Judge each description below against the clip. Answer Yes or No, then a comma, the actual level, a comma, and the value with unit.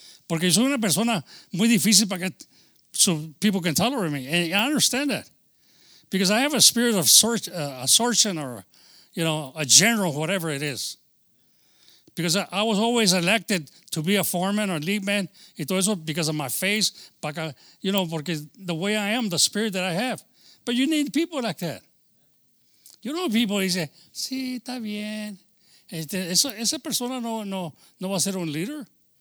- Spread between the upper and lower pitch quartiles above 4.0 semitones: Yes, average, 5.1 semitones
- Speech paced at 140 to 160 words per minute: No, average, 180 wpm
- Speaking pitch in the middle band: No, high, 195 Hz